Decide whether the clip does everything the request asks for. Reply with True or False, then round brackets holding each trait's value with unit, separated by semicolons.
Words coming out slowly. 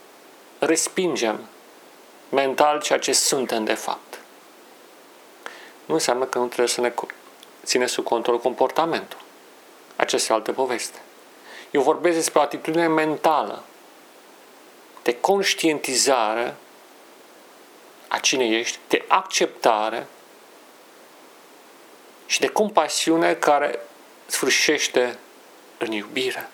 True (95 wpm)